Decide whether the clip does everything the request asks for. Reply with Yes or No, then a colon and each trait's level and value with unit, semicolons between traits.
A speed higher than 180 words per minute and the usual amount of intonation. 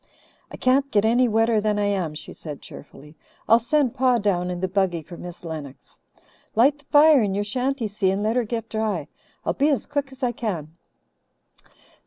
No: average, 200 wpm; wide, 5.7 semitones